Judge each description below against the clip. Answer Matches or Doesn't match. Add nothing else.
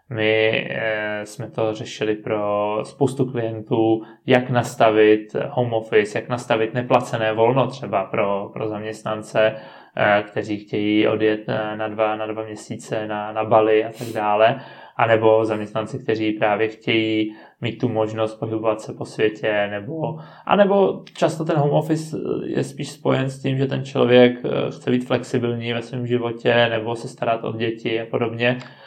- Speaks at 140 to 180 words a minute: Matches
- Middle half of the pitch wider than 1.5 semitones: Matches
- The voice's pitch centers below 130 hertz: Matches